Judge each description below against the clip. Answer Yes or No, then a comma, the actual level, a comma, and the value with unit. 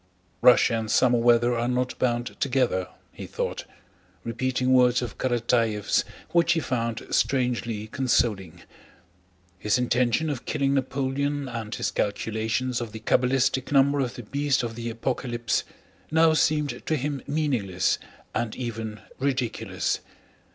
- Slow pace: Yes, slow, 130 wpm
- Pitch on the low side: Yes, low, 125 Hz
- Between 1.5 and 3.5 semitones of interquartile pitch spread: Yes, average, 2.7 semitones